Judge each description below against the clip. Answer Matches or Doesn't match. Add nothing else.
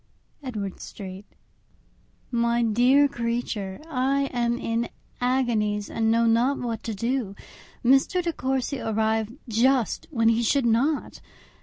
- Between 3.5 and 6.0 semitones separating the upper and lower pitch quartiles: Doesn't match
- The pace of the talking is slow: Matches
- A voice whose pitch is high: Matches